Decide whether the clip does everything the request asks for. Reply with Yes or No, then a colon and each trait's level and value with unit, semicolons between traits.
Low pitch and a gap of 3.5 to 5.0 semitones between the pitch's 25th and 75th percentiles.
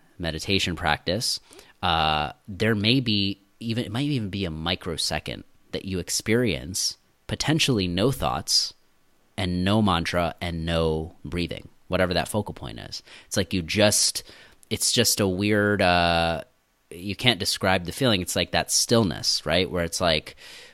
Yes: very low, 95 Hz; average, 4.3 semitones